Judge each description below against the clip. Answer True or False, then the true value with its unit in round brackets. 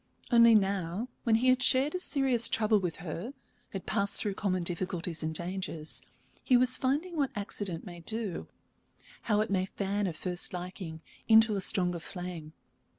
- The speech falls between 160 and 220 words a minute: True (165 wpm)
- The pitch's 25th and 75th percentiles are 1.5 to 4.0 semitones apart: False (4.7 semitones)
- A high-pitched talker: True (195 Hz)